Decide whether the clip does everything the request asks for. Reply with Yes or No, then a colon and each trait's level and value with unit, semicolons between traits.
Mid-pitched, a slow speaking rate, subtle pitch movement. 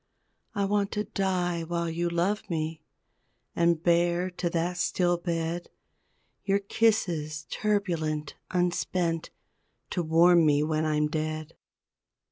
Yes: medium, 170 Hz; slow, 115 wpm; narrow, 2.2 semitones